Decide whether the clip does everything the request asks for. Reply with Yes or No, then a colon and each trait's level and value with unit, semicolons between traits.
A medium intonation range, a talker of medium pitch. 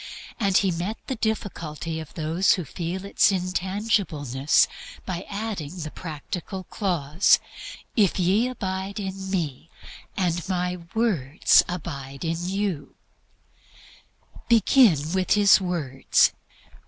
Yes: average, 3.7 semitones; medium, 180 Hz